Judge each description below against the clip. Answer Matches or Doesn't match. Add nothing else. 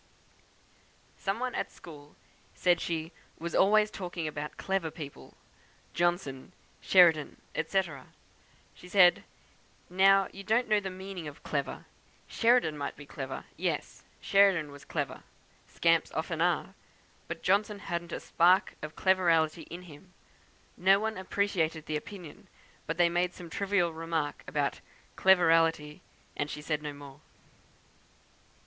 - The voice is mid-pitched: Matches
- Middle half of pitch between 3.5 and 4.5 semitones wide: Matches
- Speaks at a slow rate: Matches